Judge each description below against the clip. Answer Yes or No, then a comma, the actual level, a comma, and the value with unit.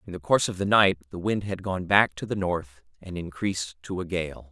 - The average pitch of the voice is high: No, very low, 90 Hz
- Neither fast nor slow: No, fast, 255 wpm